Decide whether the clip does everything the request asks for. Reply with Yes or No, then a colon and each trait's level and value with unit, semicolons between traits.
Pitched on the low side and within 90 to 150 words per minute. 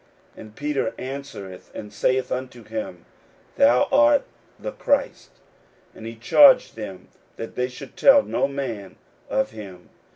Yes: low, 130 Hz; average, 140 wpm